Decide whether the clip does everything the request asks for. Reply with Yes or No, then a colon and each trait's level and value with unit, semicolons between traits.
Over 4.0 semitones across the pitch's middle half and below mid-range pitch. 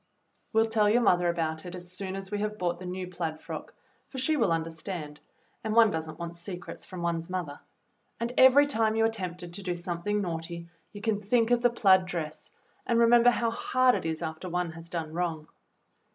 No: average, 4.6 semitones; medium, 180 Hz